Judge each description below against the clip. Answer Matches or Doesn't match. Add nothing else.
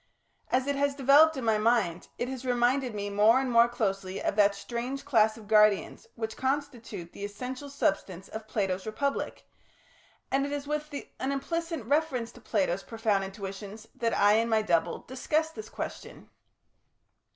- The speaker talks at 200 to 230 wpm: Doesn't match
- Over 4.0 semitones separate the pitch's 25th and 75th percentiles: Matches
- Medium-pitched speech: Doesn't match